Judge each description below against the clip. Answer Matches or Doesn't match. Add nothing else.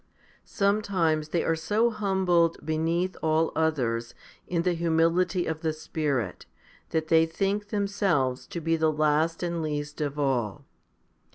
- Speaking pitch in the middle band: Matches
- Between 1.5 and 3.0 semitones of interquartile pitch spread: Matches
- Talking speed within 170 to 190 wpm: Doesn't match